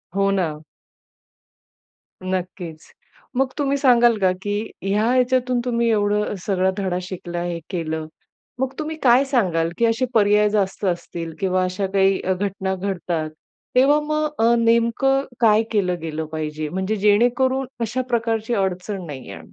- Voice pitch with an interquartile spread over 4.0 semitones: Yes, average, 4.6 semitones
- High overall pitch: Yes, high, 205 Hz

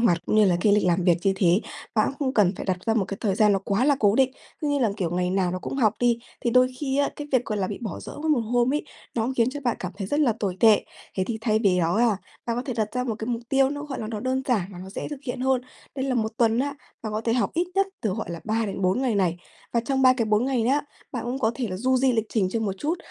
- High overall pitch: Yes, high, 225 Hz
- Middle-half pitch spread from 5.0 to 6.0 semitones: No, average, 4.4 semitones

